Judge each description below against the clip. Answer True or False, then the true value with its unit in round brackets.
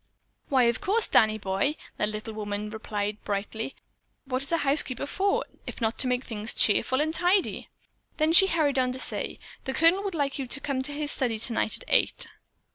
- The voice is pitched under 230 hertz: False (260 Hz)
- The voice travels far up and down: True (5.7 semitones)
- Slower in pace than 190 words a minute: False (200 wpm)